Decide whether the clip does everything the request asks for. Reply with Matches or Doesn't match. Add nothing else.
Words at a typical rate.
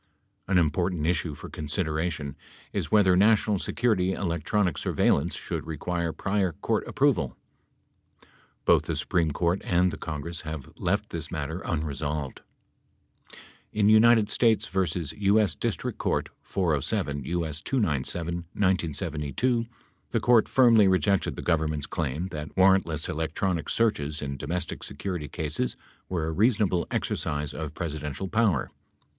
Doesn't match